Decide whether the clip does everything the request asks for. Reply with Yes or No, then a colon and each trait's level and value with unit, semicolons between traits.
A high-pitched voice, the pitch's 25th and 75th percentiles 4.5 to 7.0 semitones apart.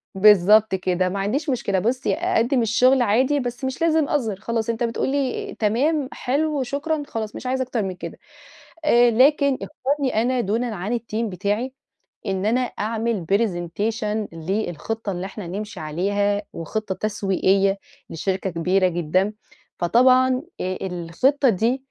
Yes: high, 220 Hz; average, 4.9 semitones